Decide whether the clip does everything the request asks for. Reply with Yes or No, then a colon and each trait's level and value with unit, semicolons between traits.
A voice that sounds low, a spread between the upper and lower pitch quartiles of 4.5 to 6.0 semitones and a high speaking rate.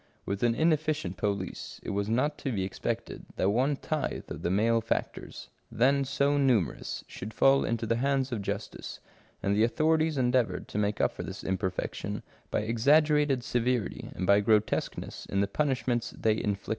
No: low, 115 Hz; average, 5.2 semitones; average, 170 wpm